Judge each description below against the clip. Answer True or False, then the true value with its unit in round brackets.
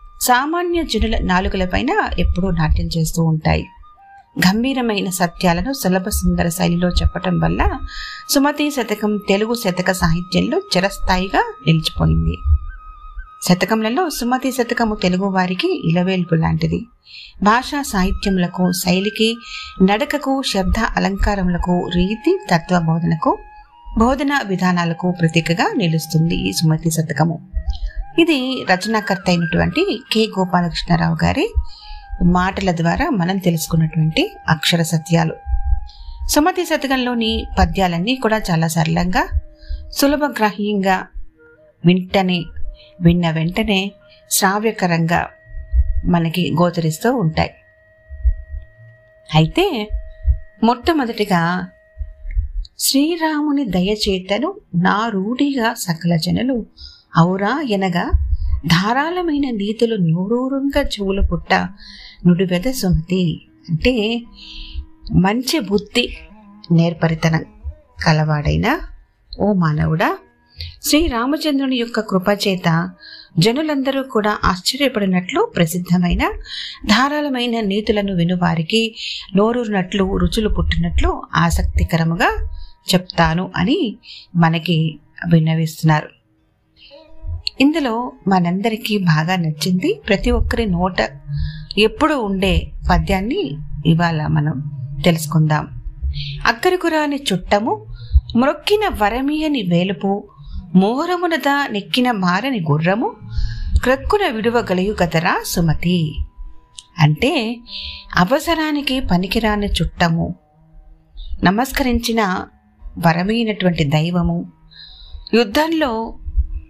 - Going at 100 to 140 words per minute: False (75 wpm)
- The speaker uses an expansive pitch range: True (6.6 semitones)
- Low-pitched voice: False (185 Hz)